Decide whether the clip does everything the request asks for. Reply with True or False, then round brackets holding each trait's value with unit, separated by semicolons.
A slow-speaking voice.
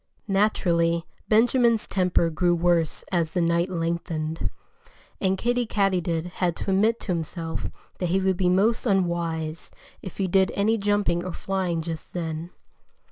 False (145 wpm)